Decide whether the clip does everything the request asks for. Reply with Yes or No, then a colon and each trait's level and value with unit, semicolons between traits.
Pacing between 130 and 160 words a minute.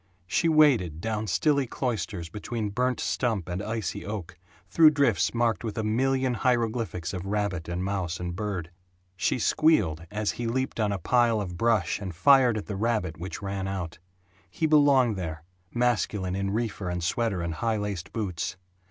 No: average, 170 wpm